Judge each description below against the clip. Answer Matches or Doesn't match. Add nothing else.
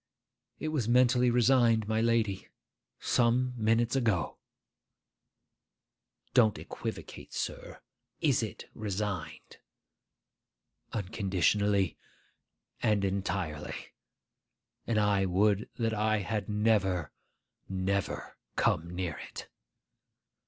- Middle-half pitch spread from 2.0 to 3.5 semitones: Matches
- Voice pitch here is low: Matches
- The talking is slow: Matches